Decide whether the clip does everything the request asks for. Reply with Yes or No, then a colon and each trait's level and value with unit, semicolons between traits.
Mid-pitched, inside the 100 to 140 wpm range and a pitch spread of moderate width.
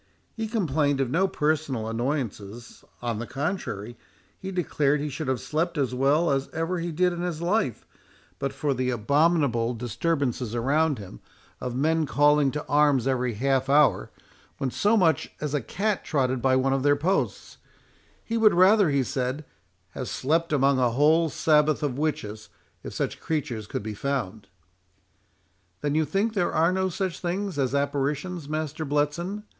No: medium, 145 Hz; average, 165 wpm; average, 4.2 semitones